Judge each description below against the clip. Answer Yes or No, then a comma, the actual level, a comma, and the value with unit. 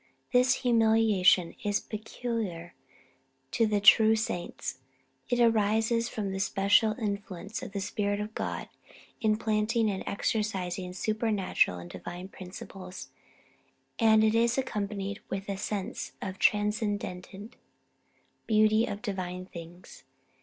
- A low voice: No, high, 210 Hz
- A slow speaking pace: Yes, slow, 120 wpm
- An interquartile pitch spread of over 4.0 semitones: No, narrow, 2.6 semitones